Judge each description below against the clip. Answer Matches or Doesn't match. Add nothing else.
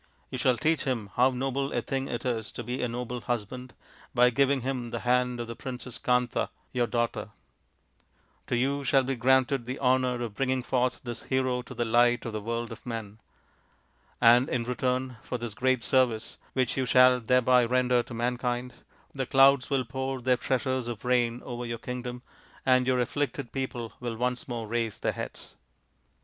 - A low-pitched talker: Matches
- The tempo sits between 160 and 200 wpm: Matches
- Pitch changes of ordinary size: Doesn't match